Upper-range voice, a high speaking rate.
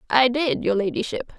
No: high, 235 Hz; average, 175 wpm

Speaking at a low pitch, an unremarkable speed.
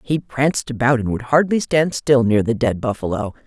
No: low, 125 Hz; fast, 210 wpm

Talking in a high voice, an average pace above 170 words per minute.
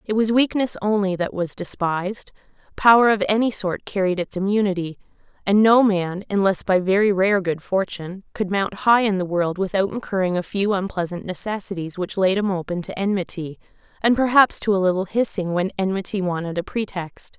Yes: high, 195 Hz; average, 180 wpm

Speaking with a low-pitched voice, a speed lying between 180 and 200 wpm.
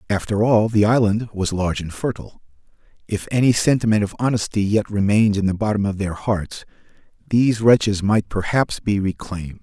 No: low, 105 Hz; average, 170 wpm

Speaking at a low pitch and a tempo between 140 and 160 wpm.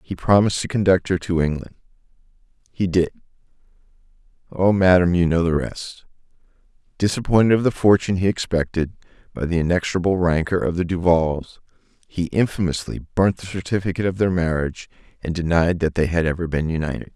Yes: very low, 90 Hz; average, 145 wpm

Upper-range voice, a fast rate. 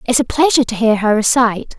Yes: high, 235 Hz; fast, 235 wpm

